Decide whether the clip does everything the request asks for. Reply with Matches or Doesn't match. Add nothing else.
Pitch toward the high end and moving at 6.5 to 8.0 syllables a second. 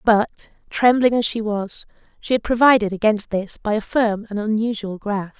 Doesn't match